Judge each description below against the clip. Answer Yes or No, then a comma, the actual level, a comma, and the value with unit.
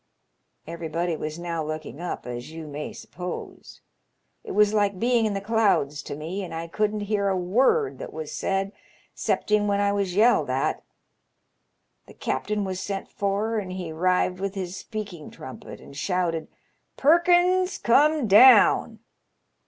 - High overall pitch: Yes, high, 195 Hz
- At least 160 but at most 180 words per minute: Yes, average, 165 wpm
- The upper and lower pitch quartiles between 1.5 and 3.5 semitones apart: No, average, 4.3 semitones